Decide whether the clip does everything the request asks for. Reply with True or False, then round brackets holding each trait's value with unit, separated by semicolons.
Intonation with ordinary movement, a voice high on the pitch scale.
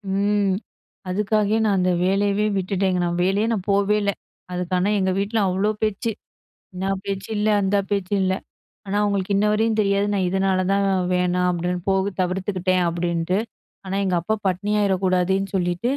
False (1.8 semitones; 195 Hz)